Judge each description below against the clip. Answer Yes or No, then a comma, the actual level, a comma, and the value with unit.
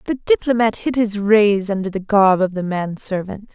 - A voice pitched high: Yes, high, 205 Hz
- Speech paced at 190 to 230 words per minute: Yes, fast, 205 wpm